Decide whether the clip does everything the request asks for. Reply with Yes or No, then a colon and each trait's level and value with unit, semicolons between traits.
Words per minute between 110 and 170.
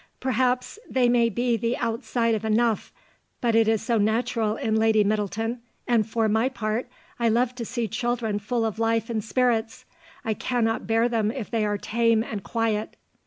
No: average, 180 wpm